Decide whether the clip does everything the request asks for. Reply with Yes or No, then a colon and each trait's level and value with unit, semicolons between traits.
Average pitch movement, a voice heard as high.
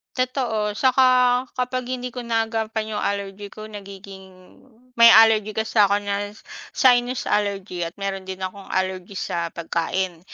Yes: average, 3.6 semitones; high, 210 Hz